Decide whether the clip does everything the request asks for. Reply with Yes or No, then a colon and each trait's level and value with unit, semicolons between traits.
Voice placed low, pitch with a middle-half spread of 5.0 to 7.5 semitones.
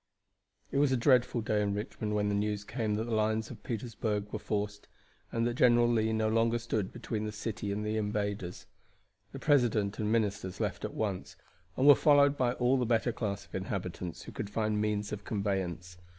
No: low, 110 Hz; narrow, 2.4 semitones